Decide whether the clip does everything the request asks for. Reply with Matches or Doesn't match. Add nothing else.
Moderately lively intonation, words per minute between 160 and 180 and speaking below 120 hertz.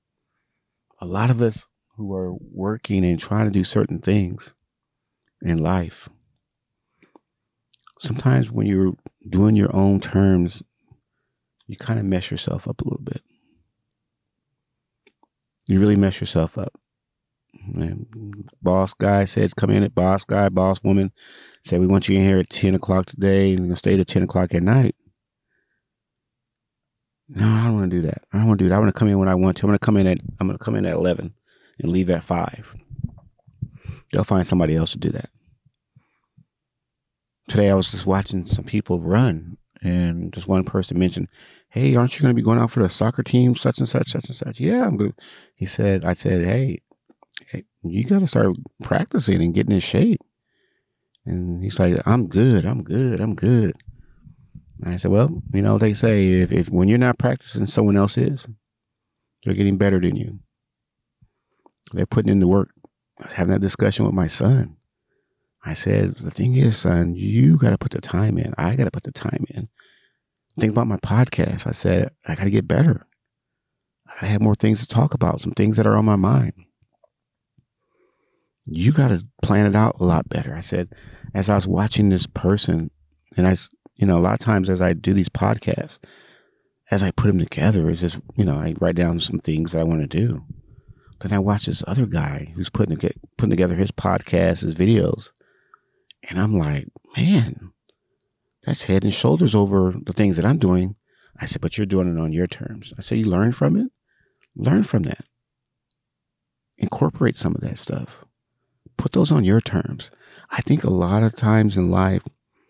Doesn't match